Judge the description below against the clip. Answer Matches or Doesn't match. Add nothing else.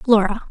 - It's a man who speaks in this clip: Doesn't match